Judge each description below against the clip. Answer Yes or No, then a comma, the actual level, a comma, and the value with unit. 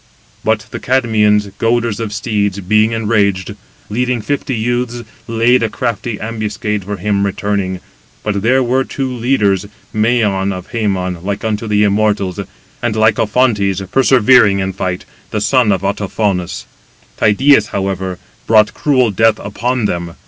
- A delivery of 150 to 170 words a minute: No, average, 140 wpm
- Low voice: Yes, low, 105 Hz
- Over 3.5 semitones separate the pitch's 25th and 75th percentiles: No, average, 2.9 semitones